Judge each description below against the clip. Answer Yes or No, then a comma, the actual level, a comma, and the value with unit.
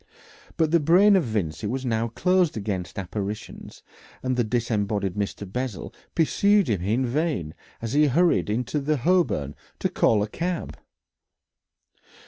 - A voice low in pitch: Yes, low, 120 Hz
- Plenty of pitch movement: Yes, wide, 7.3 semitones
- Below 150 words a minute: Yes, average, 140 wpm